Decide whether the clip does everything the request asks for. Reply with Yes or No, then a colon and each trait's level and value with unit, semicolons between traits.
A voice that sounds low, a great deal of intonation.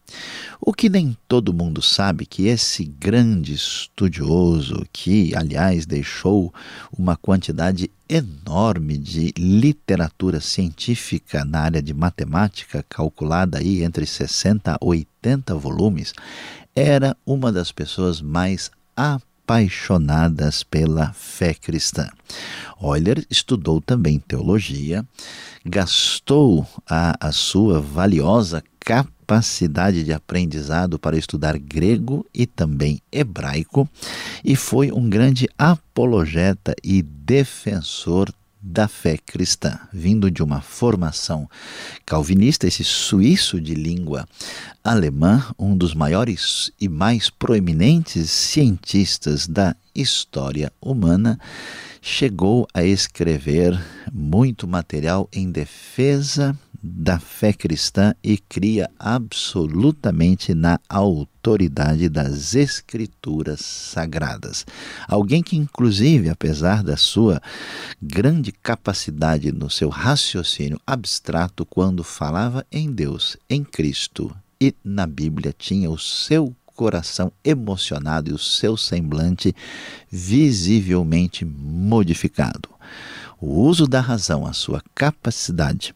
Yes: very low, 95 Hz; wide, 6.1 semitones